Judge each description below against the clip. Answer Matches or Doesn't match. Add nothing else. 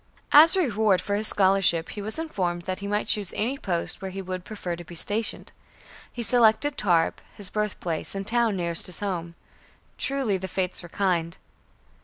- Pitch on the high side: Matches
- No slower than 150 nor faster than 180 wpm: Doesn't match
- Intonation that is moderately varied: Matches